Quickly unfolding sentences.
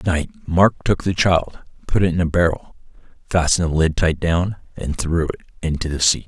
Yes: fast, 210 wpm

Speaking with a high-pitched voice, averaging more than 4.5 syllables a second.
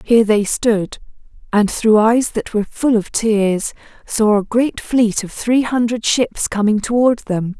No: high, 220 Hz; 4.1 syllables/s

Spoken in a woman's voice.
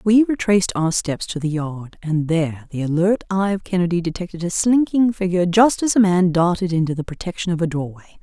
Yes: female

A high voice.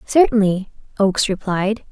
Yes: high, 200 Hz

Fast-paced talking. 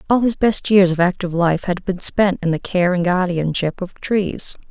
Yes: fast, 215 wpm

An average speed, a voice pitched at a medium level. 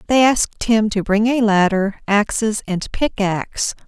No: average, 155 wpm; high, 215 Hz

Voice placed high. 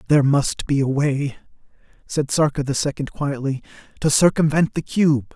No: medium, 145 Hz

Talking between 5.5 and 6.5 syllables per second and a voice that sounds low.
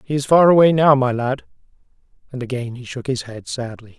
Yes: 5.7 syllables/s; low, 130 Hz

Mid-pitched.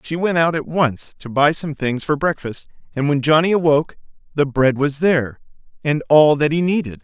Yes: medium, 150 Hz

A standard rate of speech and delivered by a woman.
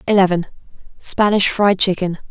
No: slow, 80 wpm; female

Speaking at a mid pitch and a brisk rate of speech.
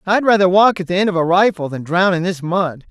Yes: medium, 180 Hz; fast, 290 wpm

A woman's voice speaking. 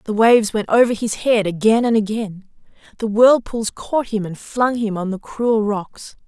Yes: female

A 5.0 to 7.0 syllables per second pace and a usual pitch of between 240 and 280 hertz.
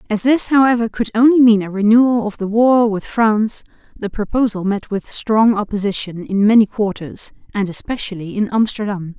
No: 5.2 syllables/s; high, 215 Hz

